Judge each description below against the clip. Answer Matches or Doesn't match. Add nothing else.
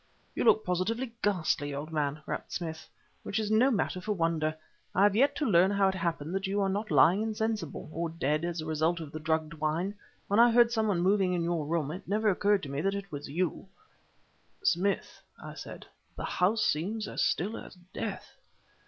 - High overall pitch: Doesn't match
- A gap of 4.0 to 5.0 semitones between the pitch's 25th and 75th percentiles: Matches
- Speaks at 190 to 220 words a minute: Matches